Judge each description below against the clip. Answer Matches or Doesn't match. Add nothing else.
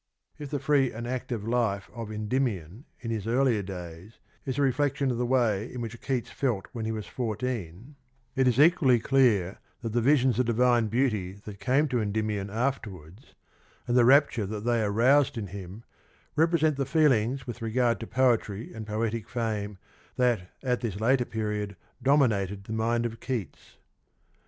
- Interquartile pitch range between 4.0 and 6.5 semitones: Doesn't match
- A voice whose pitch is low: Matches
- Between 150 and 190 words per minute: Matches